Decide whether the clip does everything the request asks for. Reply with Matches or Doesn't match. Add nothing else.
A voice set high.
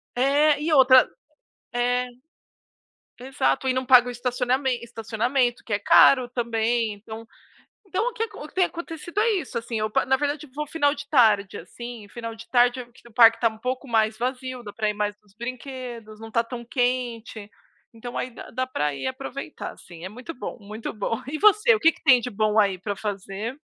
Matches